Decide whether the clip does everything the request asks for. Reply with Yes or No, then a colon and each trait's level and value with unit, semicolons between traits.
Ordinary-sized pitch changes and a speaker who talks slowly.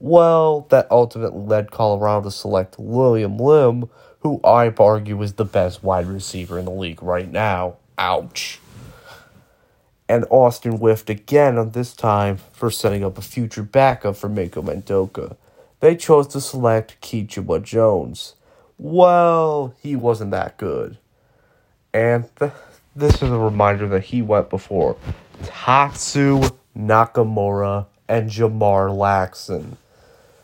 Yes: average, 3.8 semitones; slow, 130 wpm